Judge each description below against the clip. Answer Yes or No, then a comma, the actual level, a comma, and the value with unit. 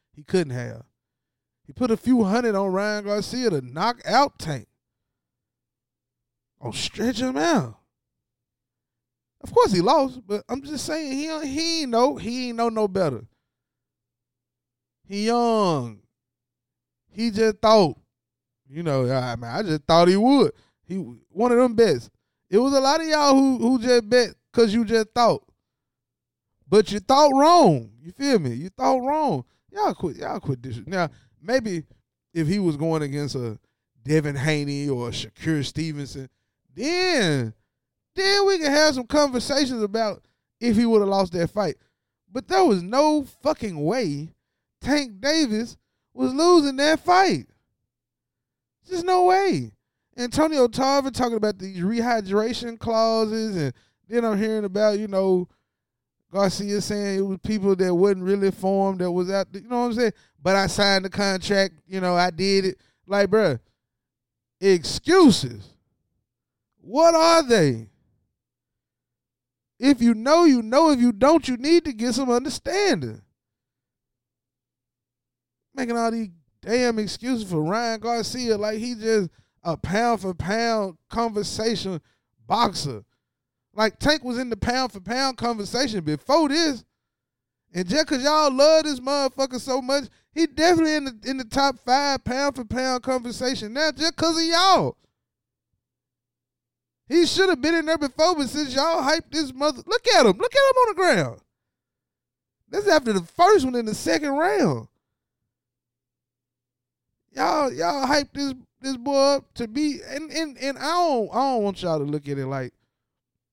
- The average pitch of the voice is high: Yes, high, 210 Hz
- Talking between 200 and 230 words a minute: No, average, 160 wpm